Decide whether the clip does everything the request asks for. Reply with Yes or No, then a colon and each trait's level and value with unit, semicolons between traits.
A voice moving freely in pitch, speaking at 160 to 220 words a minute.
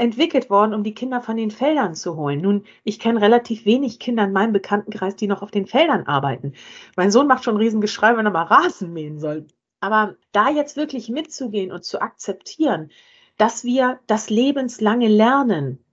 No: average, 4.1 semitones; average, 185 wpm